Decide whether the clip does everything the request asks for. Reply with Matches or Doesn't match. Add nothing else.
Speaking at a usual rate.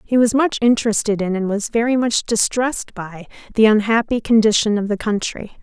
Matches